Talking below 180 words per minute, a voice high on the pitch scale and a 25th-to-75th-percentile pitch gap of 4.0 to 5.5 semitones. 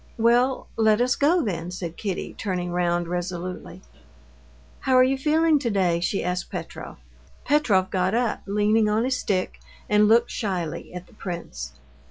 Yes: average, 155 wpm; high, 205 Hz; average, 5.1 semitones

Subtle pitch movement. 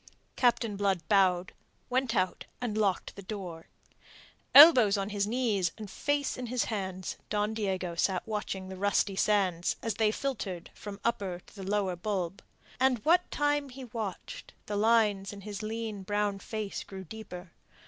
No: average, 3.0 semitones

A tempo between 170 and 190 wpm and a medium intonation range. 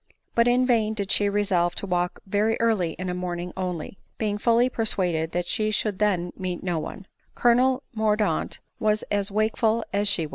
Yes: average, 185 wpm; average, 3.6 semitones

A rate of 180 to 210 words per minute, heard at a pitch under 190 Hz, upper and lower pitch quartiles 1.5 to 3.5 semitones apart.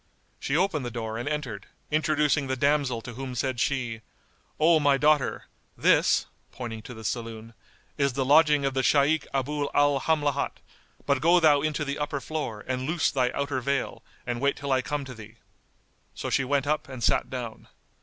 Yes: average, 185 wpm; medium, 140 Hz; average, 3.0 semitones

